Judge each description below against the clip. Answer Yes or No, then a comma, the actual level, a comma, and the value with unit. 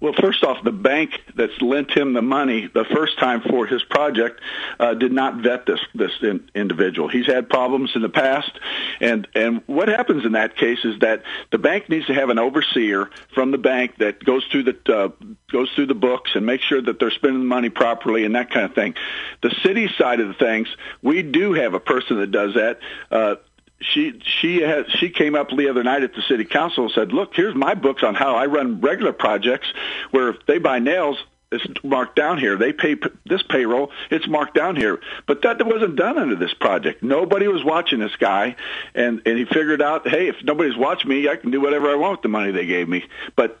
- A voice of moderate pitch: No, low, 130 Hz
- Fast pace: Yes, fast, 230 wpm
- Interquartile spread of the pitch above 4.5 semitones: No, average, 4.0 semitones